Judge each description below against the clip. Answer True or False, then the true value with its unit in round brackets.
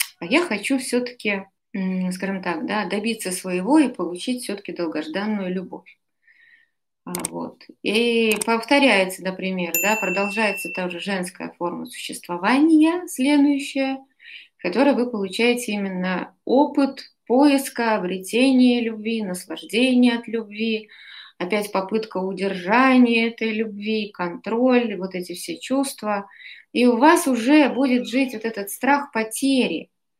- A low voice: False (225 Hz)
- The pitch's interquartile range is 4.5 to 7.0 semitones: True (5.2 semitones)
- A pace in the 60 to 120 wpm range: True (115 wpm)